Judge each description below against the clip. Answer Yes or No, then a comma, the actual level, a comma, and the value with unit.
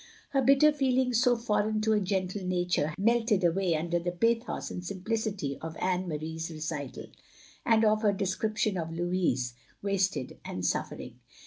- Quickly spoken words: No, average, 170 wpm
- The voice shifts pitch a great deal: No, average, 4.3 semitones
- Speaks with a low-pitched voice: No, high, 190 Hz